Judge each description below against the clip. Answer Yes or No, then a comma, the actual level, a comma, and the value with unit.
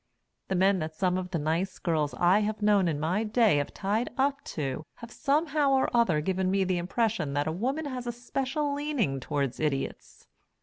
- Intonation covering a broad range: Yes, wide, 7.4 semitones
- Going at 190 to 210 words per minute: Yes, average, 200 wpm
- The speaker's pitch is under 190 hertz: No, high, 195 Hz